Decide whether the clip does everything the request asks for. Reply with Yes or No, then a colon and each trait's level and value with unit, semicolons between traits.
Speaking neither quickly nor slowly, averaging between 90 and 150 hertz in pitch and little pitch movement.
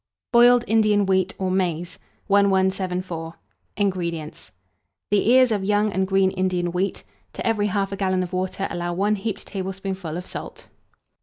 No: average, 145 wpm; high, 190 Hz; narrow, 1.9 semitones